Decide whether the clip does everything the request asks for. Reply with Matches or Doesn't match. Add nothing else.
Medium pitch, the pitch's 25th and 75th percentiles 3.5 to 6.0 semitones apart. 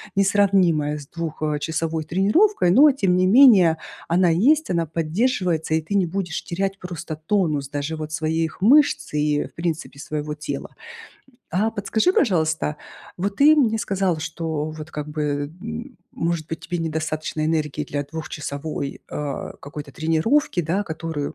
Matches